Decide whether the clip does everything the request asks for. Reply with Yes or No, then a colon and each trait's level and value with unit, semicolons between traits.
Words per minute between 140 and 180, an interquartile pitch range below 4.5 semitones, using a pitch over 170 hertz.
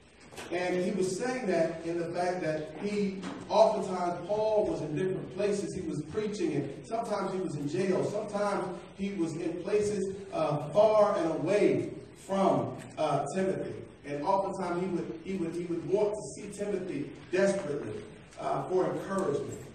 Yes: average, 160 wpm; average, 3.1 semitones; high, 190 Hz